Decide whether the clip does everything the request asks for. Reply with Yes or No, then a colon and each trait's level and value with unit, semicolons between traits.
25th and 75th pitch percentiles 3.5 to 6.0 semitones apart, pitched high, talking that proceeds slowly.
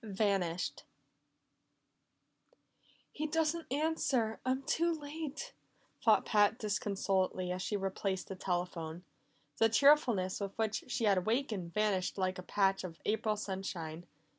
Yes: average, 5.3 semitones; high, 205 Hz; slow, 125 wpm